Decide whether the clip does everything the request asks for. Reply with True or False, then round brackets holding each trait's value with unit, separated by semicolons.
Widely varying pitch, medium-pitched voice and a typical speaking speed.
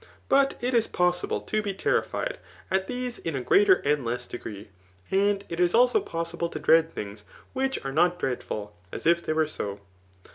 True (8.0 semitones; 175 Hz; 185 wpm)